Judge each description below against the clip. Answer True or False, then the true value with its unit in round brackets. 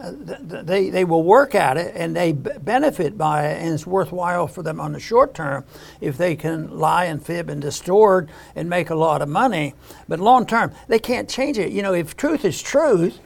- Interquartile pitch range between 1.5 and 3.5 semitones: False (3.9 semitones)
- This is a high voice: False (175 Hz)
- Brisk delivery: True (215 wpm)